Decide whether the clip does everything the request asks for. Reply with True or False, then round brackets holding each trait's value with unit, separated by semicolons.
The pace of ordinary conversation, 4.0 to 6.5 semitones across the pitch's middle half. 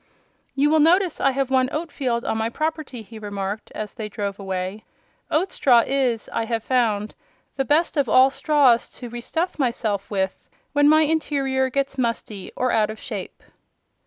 True (180 wpm; 5.0 semitones)